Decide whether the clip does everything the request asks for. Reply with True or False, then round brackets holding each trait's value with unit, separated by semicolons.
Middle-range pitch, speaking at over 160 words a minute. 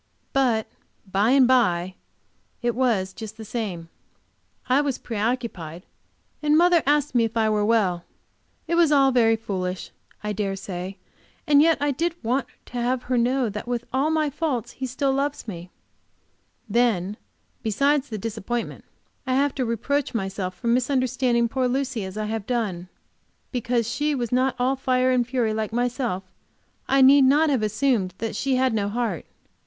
False (240 Hz; 170 wpm)